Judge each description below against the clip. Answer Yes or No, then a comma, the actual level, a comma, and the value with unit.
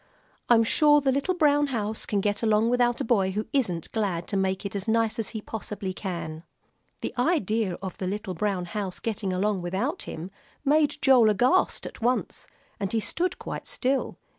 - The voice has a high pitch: Yes, high, 215 Hz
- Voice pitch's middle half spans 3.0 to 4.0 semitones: No, average, 4.6 semitones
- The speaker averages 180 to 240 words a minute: Yes, average, 190 wpm